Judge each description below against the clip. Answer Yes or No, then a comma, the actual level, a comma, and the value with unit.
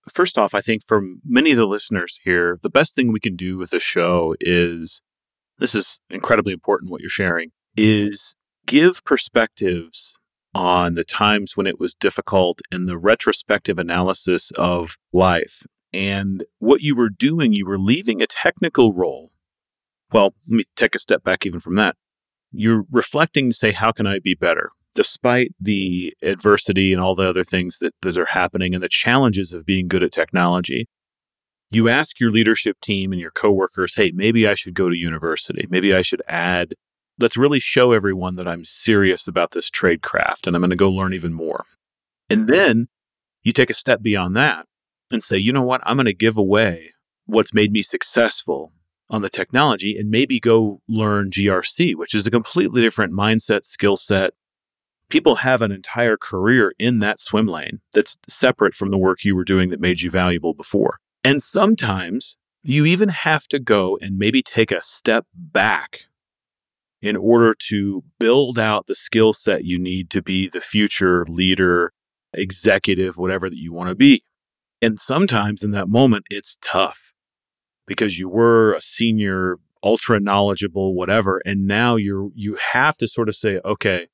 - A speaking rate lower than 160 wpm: No, average, 180 wpm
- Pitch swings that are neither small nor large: Yes, average, 3.6 semitones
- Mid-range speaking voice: No, low, 100 Hz